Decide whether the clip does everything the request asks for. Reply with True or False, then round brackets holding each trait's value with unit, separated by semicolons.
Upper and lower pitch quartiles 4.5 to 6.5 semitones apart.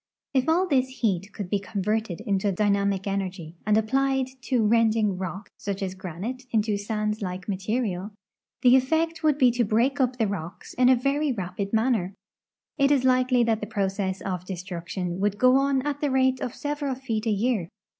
True (4.8 semitones)